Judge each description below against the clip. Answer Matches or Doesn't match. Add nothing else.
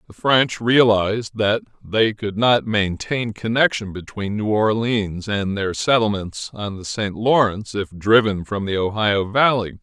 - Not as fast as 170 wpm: Matches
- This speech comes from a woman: Doesn't match